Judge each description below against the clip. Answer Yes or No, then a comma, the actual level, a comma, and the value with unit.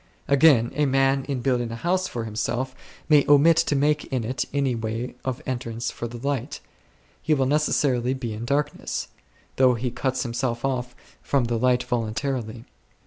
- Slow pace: No, average, 170 wpm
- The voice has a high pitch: No, low, 130 Hz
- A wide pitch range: No, average, 2.9 semitones